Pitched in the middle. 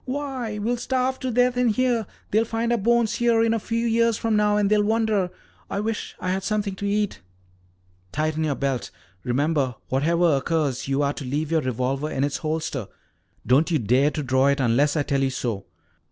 Yes: medium, 175 Hz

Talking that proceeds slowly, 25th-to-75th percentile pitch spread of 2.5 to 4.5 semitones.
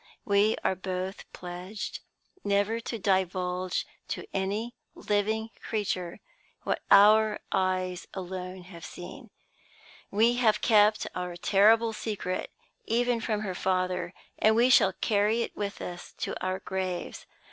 Yes: slow, 125 wpm; average, 2.9 semitones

